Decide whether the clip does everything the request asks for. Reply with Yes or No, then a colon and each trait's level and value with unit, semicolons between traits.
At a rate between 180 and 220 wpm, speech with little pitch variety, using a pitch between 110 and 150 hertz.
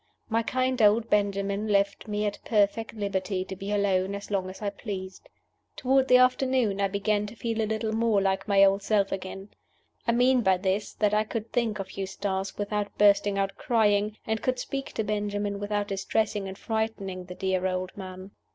No: average, 190 wpm; narrow, 2.1 semitones; high, 205 Hz